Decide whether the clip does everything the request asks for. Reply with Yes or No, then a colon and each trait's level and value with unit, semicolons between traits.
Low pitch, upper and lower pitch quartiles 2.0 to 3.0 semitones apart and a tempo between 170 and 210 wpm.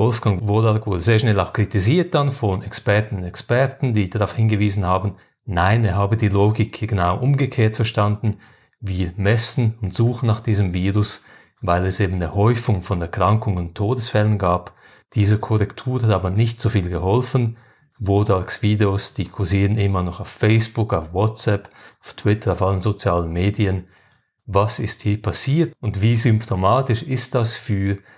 No: low, 105 Hz; narrow, 2.6 semitones; average, 160 wpm